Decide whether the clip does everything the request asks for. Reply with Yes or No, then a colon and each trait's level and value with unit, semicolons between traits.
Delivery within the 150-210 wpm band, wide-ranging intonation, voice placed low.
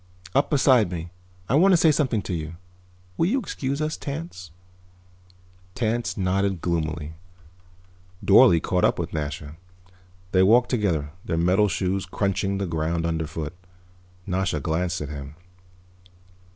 No: slow, 135 wpm; wide, 6.2 semitones; very low, 90 Hz